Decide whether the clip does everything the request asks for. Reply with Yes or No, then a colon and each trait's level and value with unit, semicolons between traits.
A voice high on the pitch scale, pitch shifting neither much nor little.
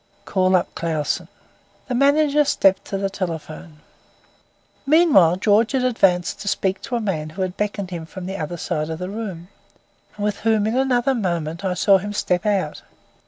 Yes: high, 195 Hz; average, 4.0 semitones